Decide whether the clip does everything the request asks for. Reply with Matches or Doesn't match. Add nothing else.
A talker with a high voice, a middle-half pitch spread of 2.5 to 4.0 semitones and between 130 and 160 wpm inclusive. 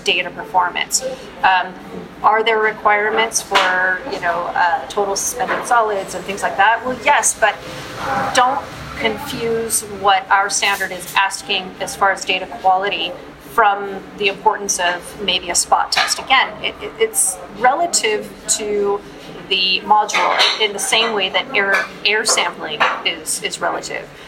Matches